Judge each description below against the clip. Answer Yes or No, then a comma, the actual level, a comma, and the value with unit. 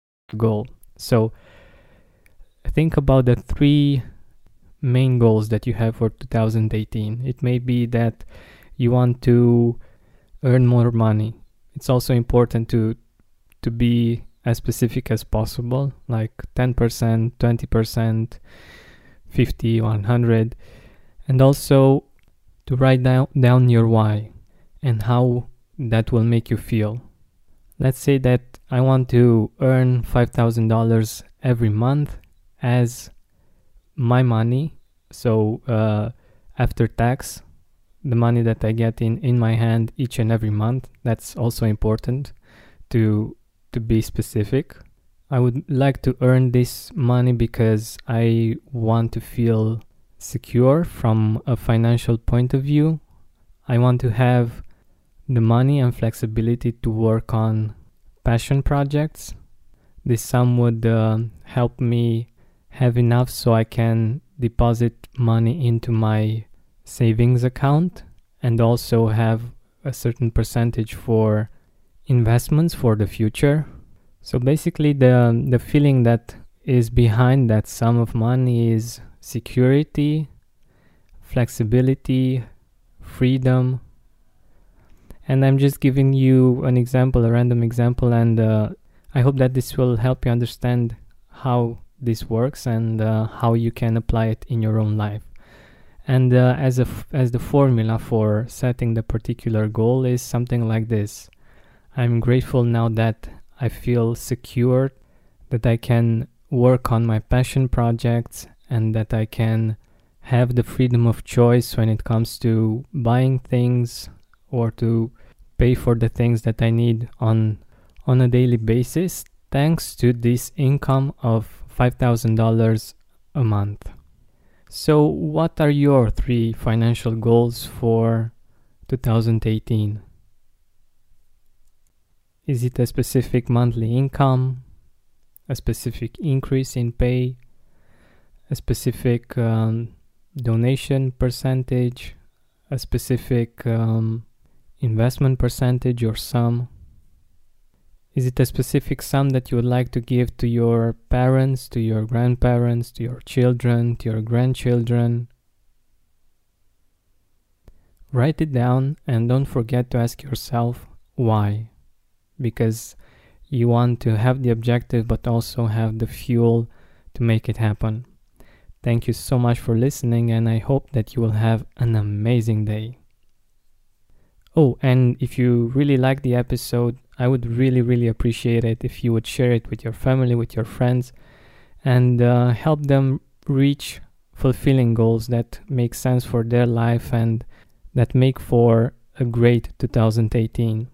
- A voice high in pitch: No, low, 120 Hz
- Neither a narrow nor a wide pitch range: No, narrow, 2.0 semitones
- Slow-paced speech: Yes, slow, 130 wpm